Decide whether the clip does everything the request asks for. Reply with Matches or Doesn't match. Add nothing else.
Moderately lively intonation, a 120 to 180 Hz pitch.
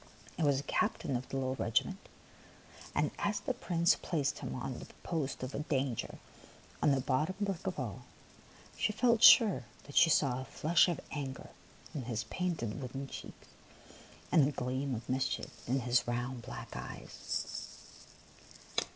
Matches